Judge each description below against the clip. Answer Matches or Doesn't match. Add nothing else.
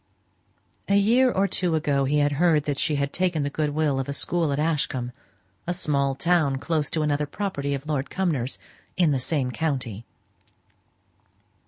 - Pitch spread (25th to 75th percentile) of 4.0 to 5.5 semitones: Doesn't match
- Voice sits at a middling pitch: Matches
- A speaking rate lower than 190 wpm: Matches